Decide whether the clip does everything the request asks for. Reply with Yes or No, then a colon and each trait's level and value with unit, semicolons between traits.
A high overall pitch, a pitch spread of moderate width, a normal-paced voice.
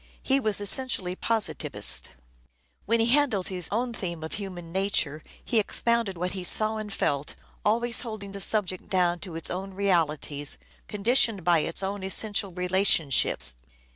Yes: high, 195 Hz; average, 3.7 semitones; average, 150 wpm